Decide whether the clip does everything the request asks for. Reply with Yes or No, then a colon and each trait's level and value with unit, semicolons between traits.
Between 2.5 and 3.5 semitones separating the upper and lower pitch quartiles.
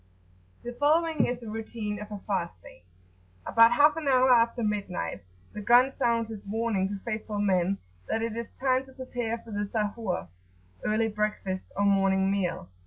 Yes: average, 3.0 semitones